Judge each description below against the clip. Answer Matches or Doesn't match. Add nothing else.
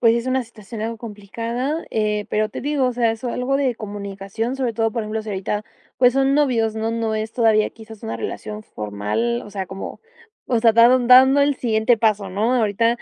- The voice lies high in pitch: Matches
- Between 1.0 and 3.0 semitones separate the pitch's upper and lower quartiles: Matches